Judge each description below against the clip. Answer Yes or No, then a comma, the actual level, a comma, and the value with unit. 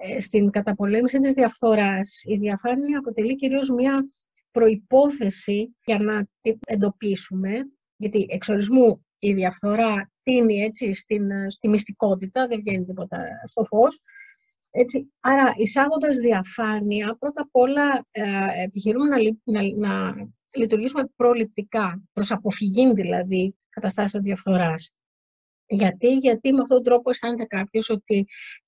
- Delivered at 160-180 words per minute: No, average, 125 wpm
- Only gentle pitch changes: No, average, 3.7 semitones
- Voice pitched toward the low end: No, high, 220 Hz